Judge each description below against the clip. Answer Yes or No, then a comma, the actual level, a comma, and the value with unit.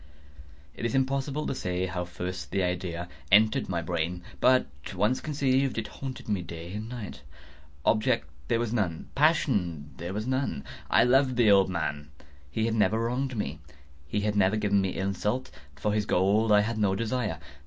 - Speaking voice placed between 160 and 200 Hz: No, low, 105 Hz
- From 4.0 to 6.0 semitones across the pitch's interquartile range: Yes, average, 5.2 semitones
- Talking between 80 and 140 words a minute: No, average, 175 wpm